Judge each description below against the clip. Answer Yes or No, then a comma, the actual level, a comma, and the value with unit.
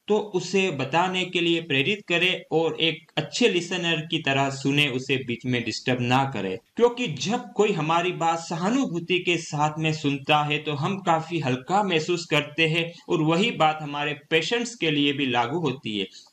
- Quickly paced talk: No, average, 180 wpm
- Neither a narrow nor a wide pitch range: Yes, average, 3.7 semitones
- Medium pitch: Yes, medium, 160 Hz